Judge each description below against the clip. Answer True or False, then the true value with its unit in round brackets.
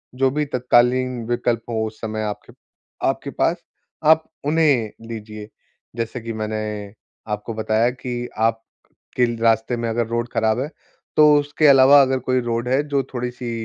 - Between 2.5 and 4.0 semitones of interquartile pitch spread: True (2.8 semitones)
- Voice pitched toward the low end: True (120 Hz)